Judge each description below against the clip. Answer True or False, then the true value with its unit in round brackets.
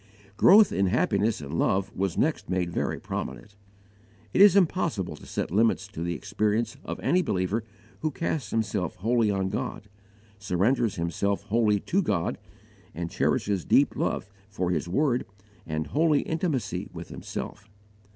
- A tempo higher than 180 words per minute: False (150 wpm)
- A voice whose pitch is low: True (105 Hz)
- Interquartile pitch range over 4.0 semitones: True (5.5 semitones)